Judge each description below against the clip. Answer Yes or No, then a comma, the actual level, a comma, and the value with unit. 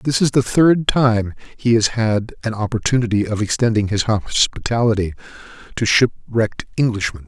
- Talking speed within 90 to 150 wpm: Yes, average, 140 wpm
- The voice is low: Yes, low, 115 Hz